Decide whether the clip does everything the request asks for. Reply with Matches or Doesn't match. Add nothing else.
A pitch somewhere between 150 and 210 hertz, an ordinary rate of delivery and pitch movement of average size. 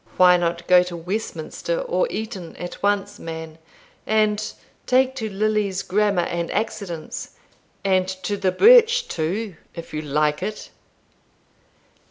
Doesn't match